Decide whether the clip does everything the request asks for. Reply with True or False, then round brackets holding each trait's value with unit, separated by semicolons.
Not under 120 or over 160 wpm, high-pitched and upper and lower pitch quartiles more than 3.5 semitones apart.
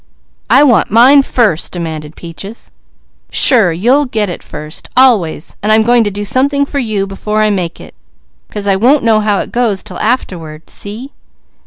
False (175 wpm; 215 Hz; 4.8 semitones)